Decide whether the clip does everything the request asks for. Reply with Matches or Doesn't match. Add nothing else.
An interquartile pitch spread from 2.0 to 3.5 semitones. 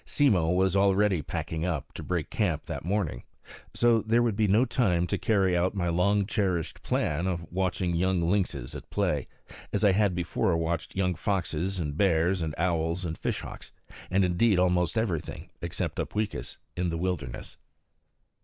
Matches